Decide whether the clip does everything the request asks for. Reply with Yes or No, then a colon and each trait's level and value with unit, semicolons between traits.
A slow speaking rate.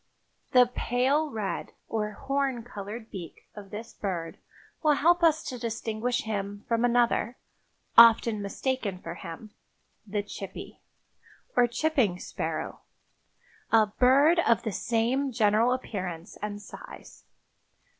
Yes: slow, 115 wpm